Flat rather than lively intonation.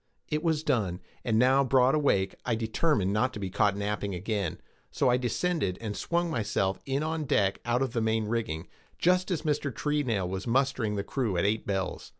No: wide, 5.5 semitones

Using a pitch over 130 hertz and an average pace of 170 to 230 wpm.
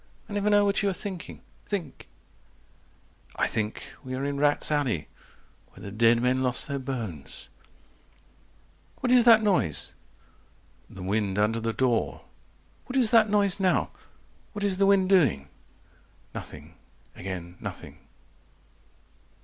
No: medium, 140 Hz; average, 140 wpm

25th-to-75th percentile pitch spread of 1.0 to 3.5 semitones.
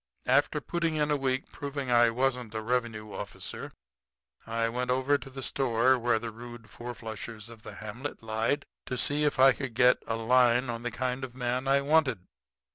Yes: average, 2.7 semitones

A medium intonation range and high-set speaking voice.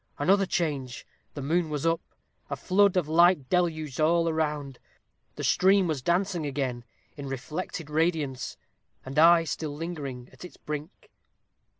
No: average, 3.3 semitones; medium, 155 Hz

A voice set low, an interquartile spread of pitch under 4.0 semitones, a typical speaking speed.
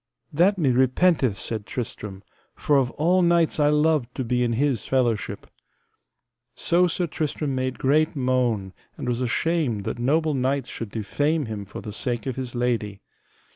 No: low, 130 Hz; average, 4.5 semitones; average, 165 wpm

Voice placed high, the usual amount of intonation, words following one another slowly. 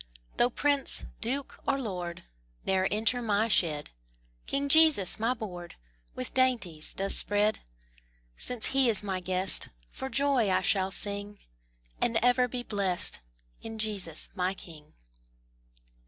Yes: high, 210 Hz; average, 4.9 semitones; slow, 130 wpm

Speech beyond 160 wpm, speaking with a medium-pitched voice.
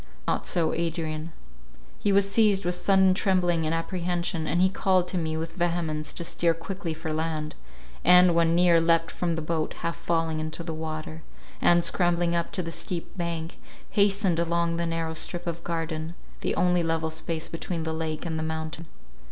Yes: average, 180 wpm; medium, 165 Hz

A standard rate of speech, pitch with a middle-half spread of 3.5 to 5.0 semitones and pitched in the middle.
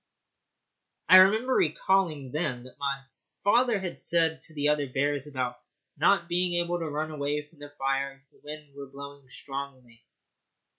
Yes: average, 160 wpm; average, 3.8 semitones; medium, 145 Hz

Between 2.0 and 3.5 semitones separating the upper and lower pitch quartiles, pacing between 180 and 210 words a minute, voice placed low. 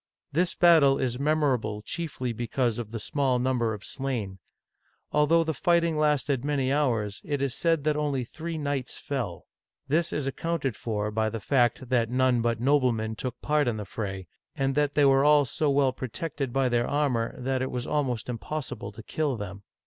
No: average, 3.9 semitones; average, 185 wpm; low, 130 Hz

